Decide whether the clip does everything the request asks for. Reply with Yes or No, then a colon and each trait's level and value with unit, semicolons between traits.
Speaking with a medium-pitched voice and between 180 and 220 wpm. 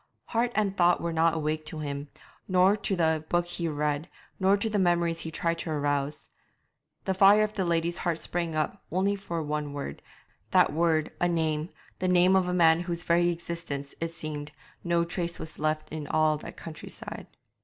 Yes: medium, 170 Hz; average, 195 wpm